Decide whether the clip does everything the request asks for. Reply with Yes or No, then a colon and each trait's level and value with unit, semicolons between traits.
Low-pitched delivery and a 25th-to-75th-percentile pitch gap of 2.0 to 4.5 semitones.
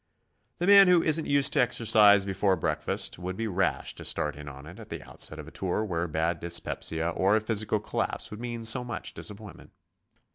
No: low, 100 Hz; average, 5.3 semitones